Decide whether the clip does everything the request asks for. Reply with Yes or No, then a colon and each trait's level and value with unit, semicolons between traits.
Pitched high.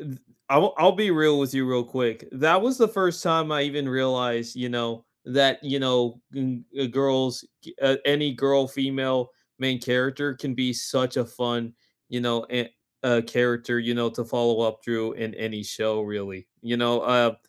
No: low, 125 Hz